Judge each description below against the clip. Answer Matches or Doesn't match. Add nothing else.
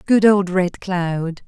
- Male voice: Doesn't match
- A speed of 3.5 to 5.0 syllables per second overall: Doesn't match